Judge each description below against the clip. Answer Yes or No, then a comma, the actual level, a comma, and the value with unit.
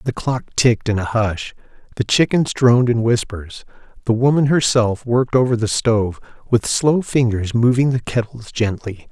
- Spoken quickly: No, average, 165 wpm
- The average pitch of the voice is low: Yes, low, 115 Hz